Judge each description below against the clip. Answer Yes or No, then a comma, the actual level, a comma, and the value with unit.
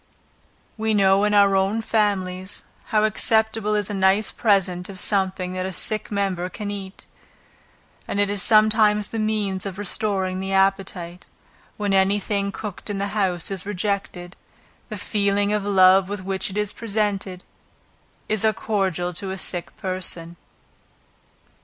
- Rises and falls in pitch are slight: Yes, narrow, 1.8 semitones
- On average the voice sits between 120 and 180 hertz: No, high, 195 Hz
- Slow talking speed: No, average, 155 wpm